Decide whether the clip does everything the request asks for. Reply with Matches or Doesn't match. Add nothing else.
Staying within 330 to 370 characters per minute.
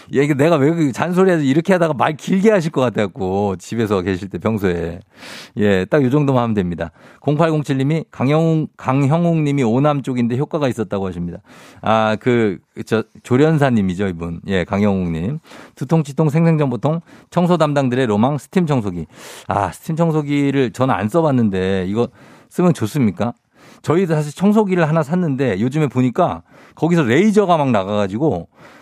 Matches